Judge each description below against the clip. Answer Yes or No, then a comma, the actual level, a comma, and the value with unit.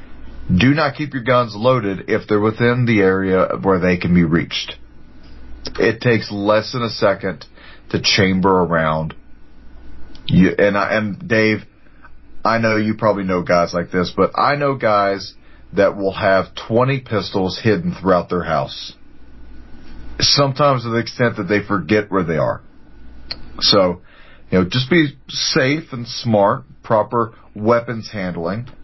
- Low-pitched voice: Yes, low, 105 Hz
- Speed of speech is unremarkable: Yes, average, 150 wpm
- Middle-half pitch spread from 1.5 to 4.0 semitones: No, average, 4.8 semitones